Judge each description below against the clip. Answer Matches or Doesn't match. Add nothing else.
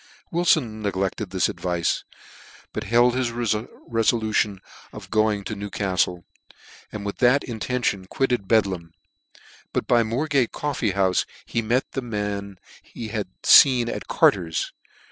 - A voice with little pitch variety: Doesn't match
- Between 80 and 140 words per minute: Matches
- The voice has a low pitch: Matches